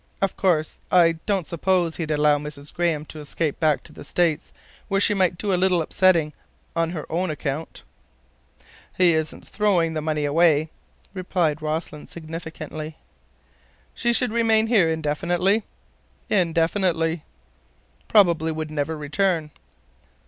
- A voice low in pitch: No, medium, 165 Hz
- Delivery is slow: Yes, slow, 130 wpm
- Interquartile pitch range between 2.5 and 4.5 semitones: Yes, average, 3.1 semitones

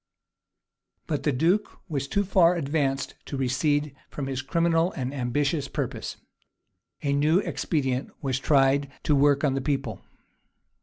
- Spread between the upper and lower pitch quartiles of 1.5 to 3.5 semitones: Yes, average, 2.7 semitones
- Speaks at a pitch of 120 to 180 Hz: Yes, medium, 140 Hz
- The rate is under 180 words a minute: Yes, average, 140 wpm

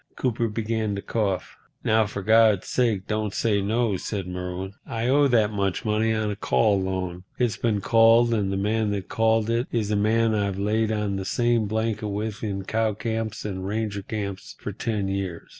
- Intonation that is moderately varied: No, narrow, 2.2 semitones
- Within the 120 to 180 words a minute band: No, average, 190 wpm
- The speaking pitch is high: No, low, 105 Hz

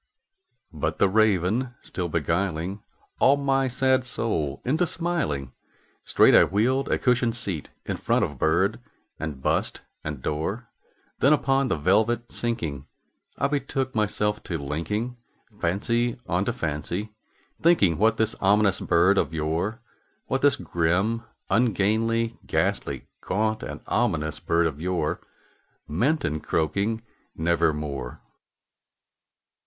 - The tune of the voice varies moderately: No, wide, 6.5 semitones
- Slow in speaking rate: Yes, slow, 125 wpm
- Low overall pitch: Yes, low, 100 Hz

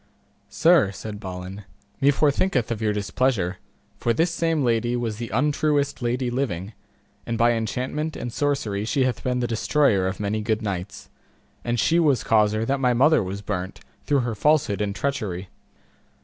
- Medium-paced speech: Yes, average, 165 wpm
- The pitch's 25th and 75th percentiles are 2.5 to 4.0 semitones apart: No, average, 5.0 semitones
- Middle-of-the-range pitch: No, low, 115 Hz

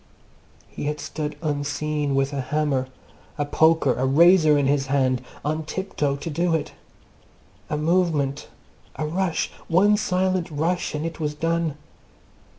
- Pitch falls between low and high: Yes, medium, 150 Hz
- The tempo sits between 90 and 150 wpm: Yes, average, 145 wpm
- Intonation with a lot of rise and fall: No, average, 2.7 semitones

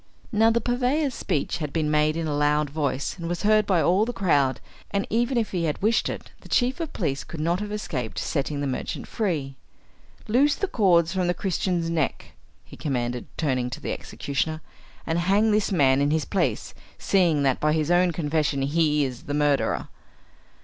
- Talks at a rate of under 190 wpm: No, average, 195 wpm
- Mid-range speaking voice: Yes, medium, 165 Hz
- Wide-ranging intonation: Yes, wide, 5.7 semitones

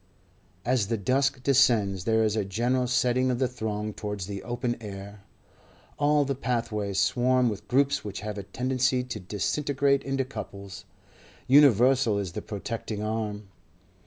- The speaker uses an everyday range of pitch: Yes, average, 3.8 semitones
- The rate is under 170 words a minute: Yes, average, 150 wpm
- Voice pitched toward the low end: Yes, low, 115 Hz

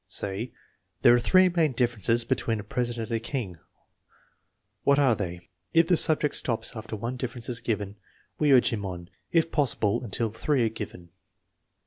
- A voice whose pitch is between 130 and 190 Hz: No, low, 115 Hz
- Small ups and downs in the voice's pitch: No, average, 3.9 semitones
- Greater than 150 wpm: Yes, average, 190 wpm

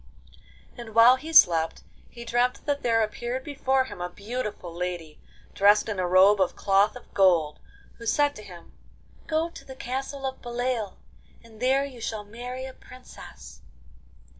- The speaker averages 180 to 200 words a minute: No, average, 165 wpm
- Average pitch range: Yes, average, 4.9 semitones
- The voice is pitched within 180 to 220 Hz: No, high, 230 Hz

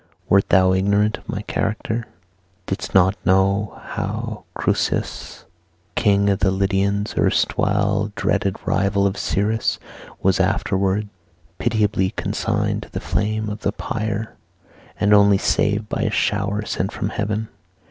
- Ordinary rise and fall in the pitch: No, narrow, 1.3 semitones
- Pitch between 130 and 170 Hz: No, low, 100 Hz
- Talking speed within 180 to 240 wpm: No, slow, 135 wpm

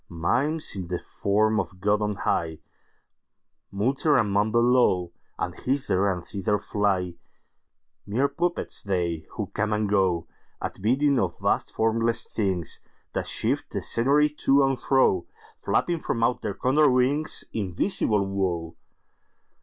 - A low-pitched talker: Yes, low, 105 Hz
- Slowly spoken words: Yes, slow, 115 wpm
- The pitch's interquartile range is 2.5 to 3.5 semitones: No, wide, 5.4 semitones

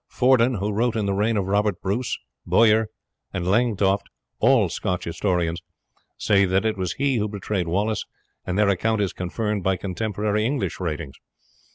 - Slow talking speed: No, average, 165 wpm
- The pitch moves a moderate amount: Yes, average, 3.0 semitones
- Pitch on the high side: No, low, 105 Hz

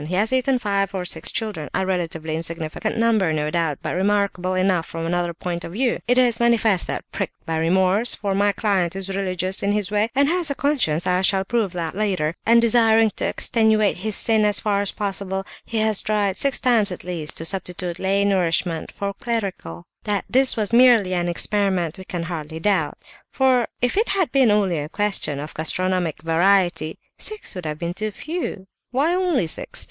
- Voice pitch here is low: No, high, 195 Hz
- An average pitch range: Yes, average, 4.1 semitones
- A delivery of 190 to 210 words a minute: Yes, average, 195 wpm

